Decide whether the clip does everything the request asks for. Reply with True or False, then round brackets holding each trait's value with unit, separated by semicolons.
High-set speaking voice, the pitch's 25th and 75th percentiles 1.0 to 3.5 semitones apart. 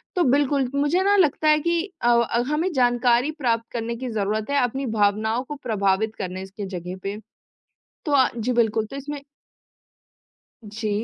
False (240 Hz; 4.9 semitones)